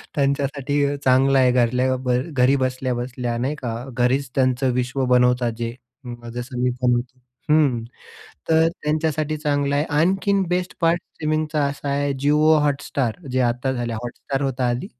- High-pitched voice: No, low, 135 Hz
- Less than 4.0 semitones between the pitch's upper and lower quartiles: Yes, average, 2.9 semitones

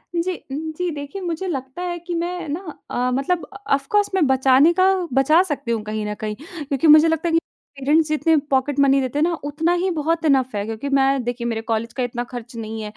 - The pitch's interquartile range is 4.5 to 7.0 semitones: Yes, average, 4.8 semitones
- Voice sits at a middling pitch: No, very high, 285 Hz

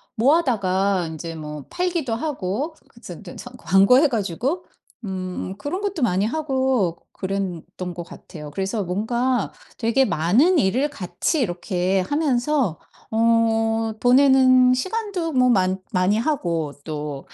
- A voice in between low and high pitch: No, high, 225 Hz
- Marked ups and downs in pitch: Yes, wide, 6.6 semitones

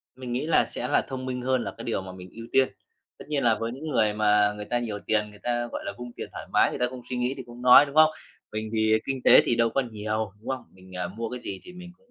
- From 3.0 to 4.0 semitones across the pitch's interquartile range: Yes, average, 3.4 semitones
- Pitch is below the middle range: Yes, low, 120 Hz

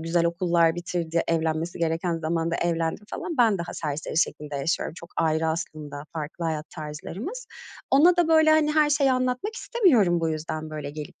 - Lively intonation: Yes, wide, 8.0 semitones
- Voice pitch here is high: No, medium, 170 Hz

